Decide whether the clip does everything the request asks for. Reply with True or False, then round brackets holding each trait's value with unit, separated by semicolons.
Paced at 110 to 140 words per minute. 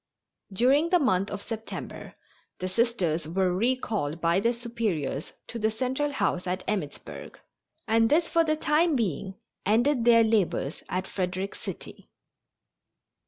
True (135 wpm)